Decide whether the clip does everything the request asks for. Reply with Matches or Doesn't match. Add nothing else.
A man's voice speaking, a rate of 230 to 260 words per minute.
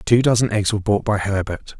Matches